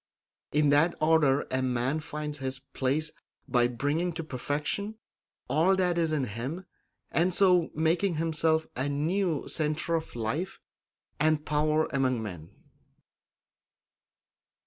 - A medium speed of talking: No, slow, 125 wpm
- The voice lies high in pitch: No, medium, 155 Hz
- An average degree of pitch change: Yes, average, 3.5 semitones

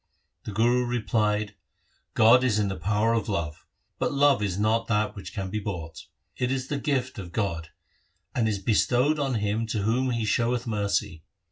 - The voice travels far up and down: No, average, 3.3 semitones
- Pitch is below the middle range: Yes, low, 110 Hz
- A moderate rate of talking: Yes, average, 190 wpm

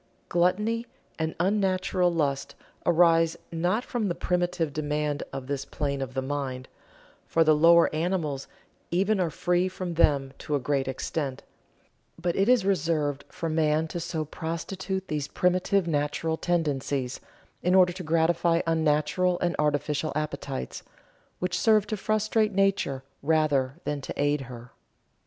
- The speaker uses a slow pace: No, average, 145 wpm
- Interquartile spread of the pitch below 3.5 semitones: No, average, 3.8 semitones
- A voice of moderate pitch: Yes, medium, 165 Hz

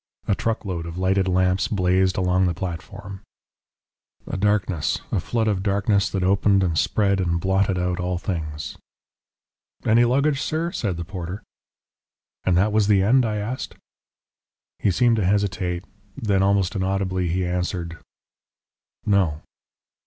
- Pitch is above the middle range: No, very low, 95 Hz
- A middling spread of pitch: No, narrow, 2.3 semitones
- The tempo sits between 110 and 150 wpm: Yes, average, 140 wpm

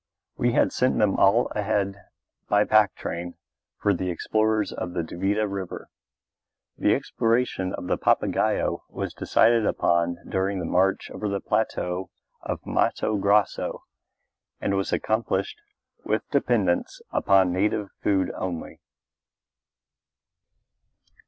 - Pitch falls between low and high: No, low, 100 Hz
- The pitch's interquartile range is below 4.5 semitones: Yes, narrow, 2.6 semitones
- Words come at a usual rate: No, slow, 120 wpm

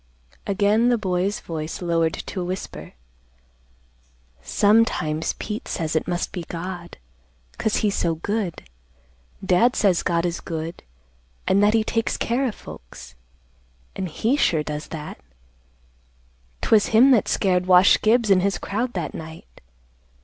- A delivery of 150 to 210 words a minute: No, average, 140 wpm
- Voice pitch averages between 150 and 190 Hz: Yes, medium, 185 Hz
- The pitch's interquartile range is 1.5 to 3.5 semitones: No, average, 4.4 semitones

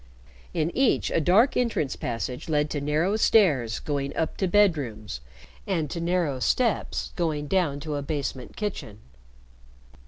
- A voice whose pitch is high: No, medium, 155 Hz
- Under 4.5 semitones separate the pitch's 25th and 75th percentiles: No, average, 5.0 semitones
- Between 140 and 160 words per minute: Yes, average, 145 wpm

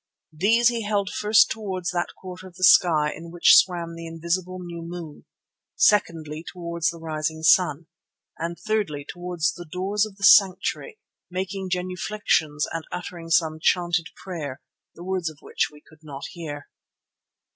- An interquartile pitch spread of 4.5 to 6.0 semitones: No, narrow, 2.6 semitones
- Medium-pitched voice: Yes, medium, 175 Hz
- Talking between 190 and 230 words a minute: No, average, 155 wpm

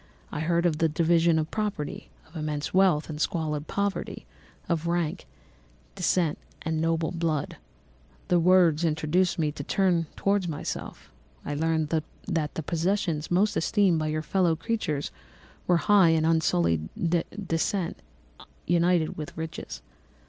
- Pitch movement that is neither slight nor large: No, narrow, 2.3 semitones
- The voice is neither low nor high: Yes, medium, 165 Hz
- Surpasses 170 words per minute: No, slow, 135 wpm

